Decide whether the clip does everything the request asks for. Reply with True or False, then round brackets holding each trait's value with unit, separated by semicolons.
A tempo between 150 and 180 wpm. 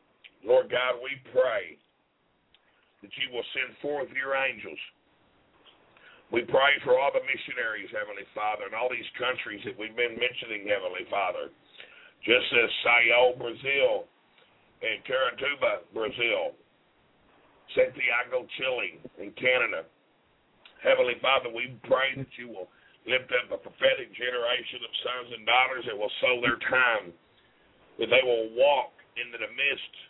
False (135 wpm)